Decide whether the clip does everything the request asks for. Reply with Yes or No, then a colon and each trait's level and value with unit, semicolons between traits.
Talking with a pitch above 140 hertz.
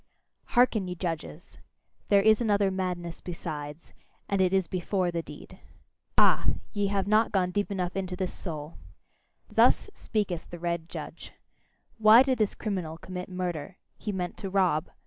Yes: medium, 185 Hz